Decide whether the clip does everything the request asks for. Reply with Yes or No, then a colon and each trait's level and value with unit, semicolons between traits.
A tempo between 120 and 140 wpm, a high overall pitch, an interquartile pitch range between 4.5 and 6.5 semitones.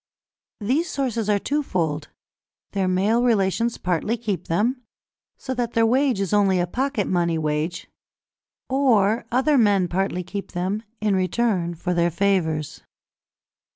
Yes: slow, 135 wpm; high, 200 Hz; average, 5.0 semitones